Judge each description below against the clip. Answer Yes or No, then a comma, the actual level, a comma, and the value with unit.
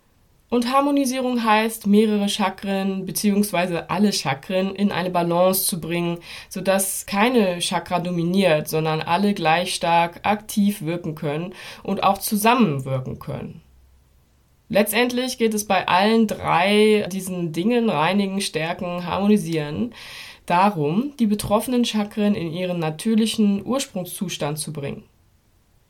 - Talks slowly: Yes, slow, 115 wpm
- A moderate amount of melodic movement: Yes, average, 3.8 semitones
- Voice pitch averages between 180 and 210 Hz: Yes, high, 190 Hz